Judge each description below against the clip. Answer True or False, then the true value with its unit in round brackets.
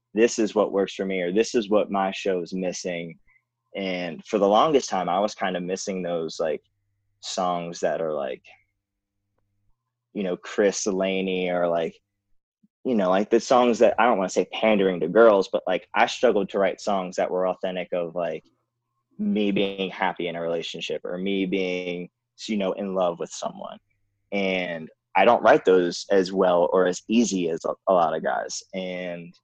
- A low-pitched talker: True (95 Hz)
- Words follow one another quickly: False (190 wpm)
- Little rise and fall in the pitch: True (1.9 semitones)